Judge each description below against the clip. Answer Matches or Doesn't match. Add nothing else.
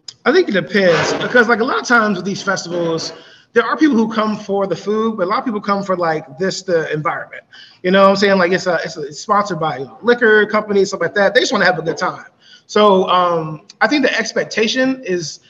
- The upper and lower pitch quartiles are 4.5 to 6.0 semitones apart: Doesn't match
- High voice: Matches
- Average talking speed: Doesn't match